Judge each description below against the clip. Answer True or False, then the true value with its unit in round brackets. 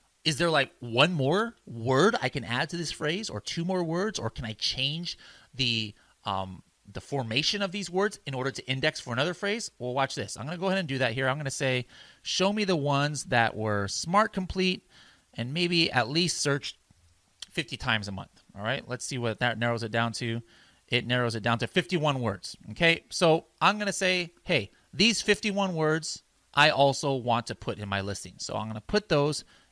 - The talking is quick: True (220 wpm)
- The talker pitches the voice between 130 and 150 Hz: True (135 Hz)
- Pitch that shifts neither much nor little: False (6.8 semitones)